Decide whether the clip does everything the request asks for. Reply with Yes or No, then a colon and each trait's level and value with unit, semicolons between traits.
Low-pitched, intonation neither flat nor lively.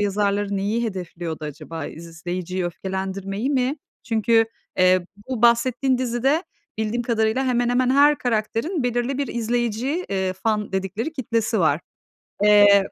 No: high, 220 Hz; average, 4.4 semitones